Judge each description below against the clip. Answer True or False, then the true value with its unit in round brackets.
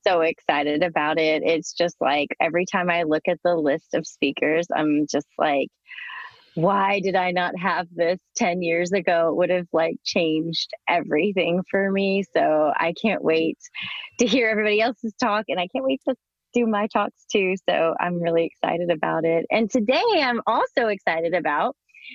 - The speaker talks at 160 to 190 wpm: True (180 wpm)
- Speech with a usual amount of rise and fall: True (4.3 semitones)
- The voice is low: False (180 Hz)